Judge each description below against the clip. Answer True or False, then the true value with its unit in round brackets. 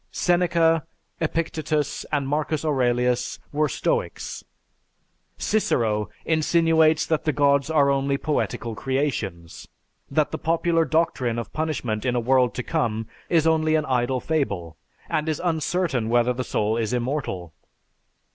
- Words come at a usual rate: False (130 wpm)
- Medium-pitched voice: True (145 Hz)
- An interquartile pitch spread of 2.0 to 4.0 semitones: False (4.7 semitones)